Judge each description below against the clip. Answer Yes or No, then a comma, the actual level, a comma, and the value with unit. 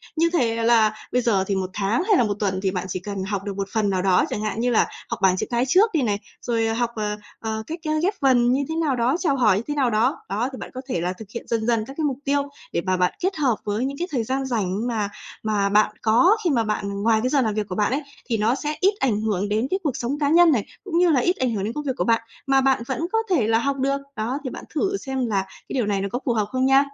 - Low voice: No, high, 235 Hz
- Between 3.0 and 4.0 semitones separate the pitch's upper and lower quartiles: No, average, 4.7 semitones